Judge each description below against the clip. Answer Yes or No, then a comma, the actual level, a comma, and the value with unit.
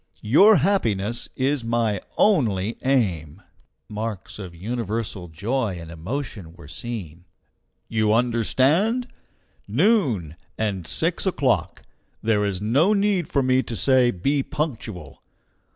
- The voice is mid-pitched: No, low, 115 Hz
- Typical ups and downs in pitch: No, wide, 5.8 semitones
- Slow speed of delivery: Yes, slow, 105 wpm